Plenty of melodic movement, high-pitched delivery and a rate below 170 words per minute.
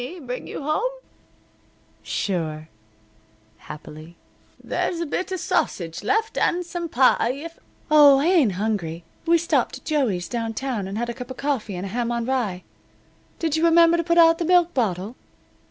No: wide, 8.7 semitones; very high, 260 Hz; average, 175 wpm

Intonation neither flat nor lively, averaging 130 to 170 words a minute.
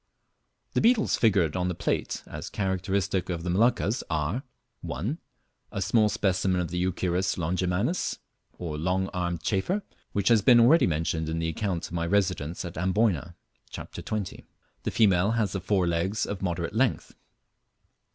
Yes: average, 3.3 semitones; average, 160 wpm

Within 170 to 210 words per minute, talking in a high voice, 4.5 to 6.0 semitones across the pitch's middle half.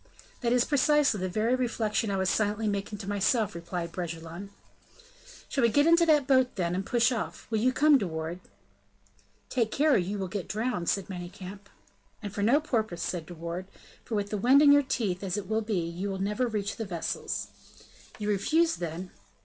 Yes: average, 200 wpm; high, 205 Hz; average, 5.0 semitones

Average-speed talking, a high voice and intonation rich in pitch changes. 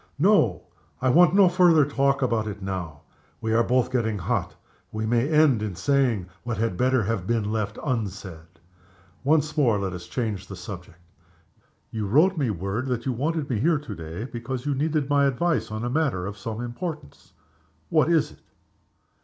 No: average, 180 wpm; low, 120 Hz; wide, 5.7 semitones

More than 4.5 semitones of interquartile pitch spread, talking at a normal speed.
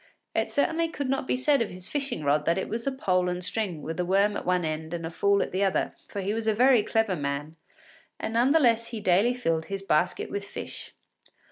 No: average, 5.1 semitones; fast, 245 wpm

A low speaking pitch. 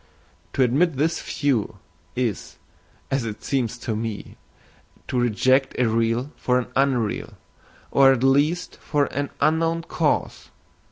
Yes: low, 130 Hz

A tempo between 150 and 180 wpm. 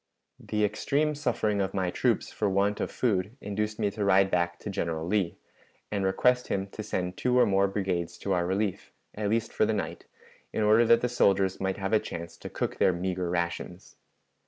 No: fast, 205 wpm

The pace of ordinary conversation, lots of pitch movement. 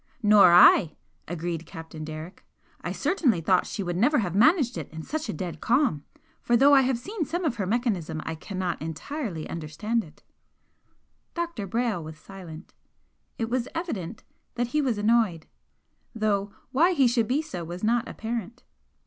Yes: average, 165 wpm; wide, 6.8 semitones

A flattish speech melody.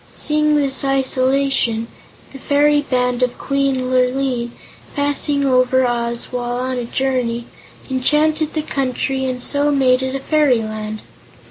Yes: narrow, 2.1 semitones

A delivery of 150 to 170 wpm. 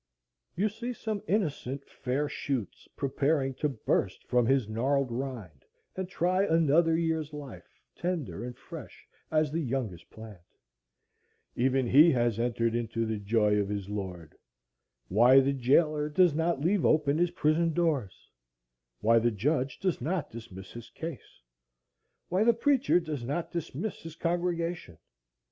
No: average, 140 wpm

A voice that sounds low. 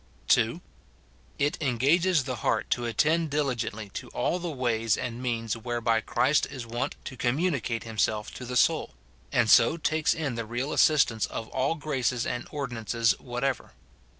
Yes: low, 125 Hz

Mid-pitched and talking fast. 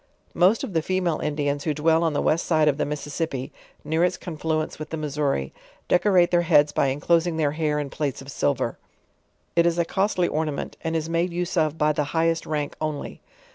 Yes: medium, 155 Hz; fast, 210 wpm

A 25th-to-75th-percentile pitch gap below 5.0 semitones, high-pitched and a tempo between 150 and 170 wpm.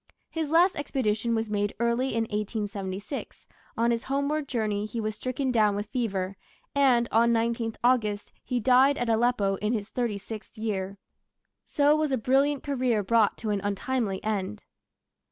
Yes: average, 3.6 semitones; high, 230 Hz; average, 160 wpm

